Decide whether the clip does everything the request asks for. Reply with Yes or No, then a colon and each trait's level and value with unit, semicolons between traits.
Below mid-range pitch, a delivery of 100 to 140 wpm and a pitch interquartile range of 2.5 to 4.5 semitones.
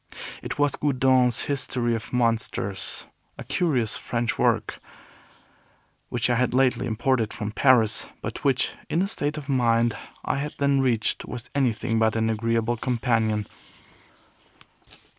Yes: low, 120 Hz; slow, 135 wpm; average, 2.8 semitones